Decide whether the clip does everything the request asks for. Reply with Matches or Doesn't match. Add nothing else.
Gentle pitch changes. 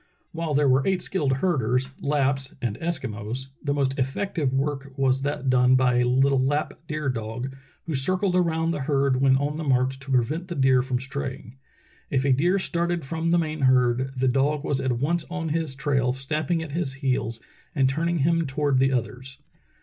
Doesn't match